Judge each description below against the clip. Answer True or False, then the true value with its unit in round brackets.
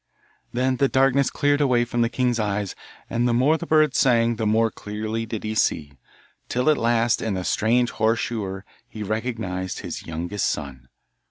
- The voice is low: True (115 Hz)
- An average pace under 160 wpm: False (180 wpm)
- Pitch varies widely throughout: False (3.1 semitones)